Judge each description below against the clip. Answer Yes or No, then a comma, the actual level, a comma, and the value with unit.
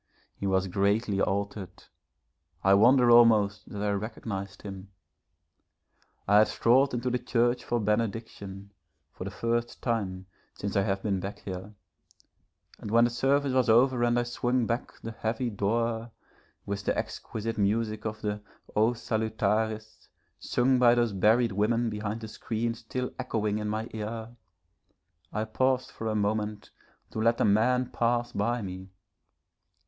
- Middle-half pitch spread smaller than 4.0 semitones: Yes, narrow, 2.6 semitones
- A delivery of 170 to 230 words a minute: No, average, 150 wpm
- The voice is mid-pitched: No, low, 110 Hz